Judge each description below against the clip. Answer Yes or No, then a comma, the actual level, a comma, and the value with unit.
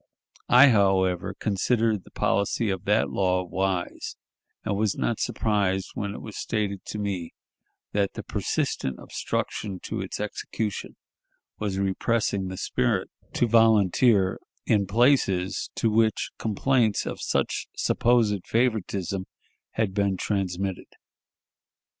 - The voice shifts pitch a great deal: No, average, 2.8 semitones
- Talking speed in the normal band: No, slow, 120 wpm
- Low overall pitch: Yes, low, 100 Hz